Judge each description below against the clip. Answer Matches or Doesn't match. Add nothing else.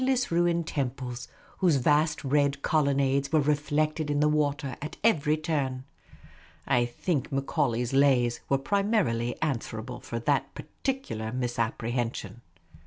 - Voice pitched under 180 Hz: Matches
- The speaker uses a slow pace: Matches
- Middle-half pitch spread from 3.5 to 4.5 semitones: Matches